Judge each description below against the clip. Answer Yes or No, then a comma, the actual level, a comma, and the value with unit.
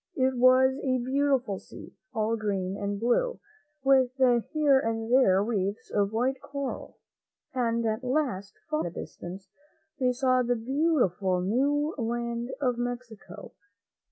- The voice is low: No, high, 240 Hz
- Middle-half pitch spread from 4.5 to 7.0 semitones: No, average, 4.1 semitones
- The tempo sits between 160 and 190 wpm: No, slow, 135 wpm